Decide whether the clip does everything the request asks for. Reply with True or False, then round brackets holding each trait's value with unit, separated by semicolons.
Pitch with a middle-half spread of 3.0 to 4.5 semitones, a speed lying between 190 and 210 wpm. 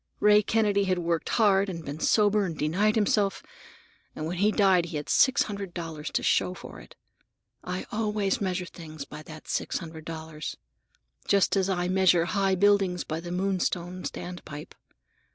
False (3.4 semitones; 170 wpm)